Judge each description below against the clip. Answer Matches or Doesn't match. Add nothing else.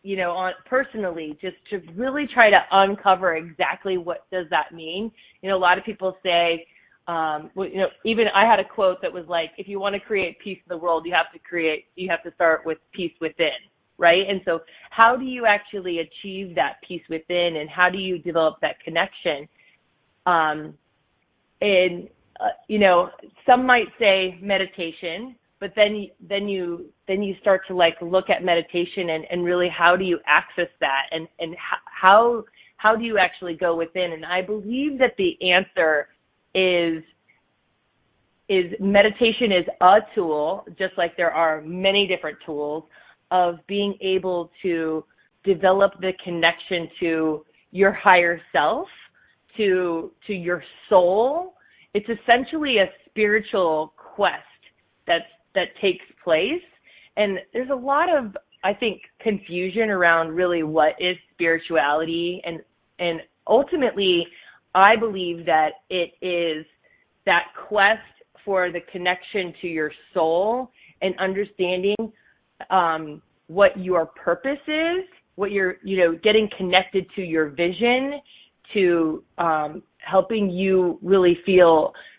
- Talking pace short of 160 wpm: Matches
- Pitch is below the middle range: Doesn't match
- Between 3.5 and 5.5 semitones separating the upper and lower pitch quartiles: Doesn't match